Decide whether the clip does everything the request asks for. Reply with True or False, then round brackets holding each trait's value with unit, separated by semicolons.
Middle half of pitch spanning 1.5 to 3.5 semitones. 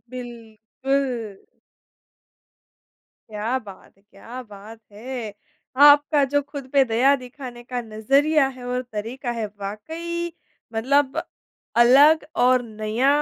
False (4.0 semitones)